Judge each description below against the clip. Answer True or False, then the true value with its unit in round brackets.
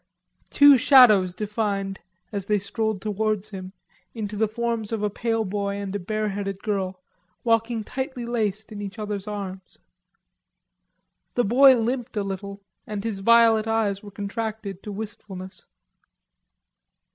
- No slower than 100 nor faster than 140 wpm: True (135 wpm)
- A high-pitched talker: True (210 Hz)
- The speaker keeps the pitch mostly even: True (2.2 semitones)